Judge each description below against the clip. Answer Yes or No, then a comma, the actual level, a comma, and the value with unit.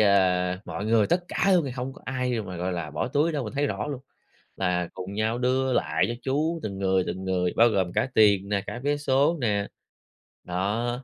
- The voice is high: No, low, 110 Hz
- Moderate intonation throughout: No, wide, 5.9 semitones